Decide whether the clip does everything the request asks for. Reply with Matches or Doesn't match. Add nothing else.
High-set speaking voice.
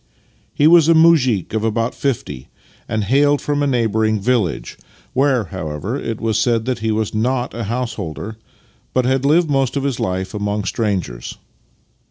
Doesn't match